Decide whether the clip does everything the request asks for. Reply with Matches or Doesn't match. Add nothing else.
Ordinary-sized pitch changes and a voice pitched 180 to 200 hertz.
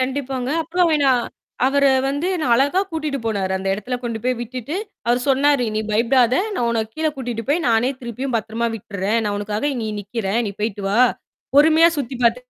Doesn't match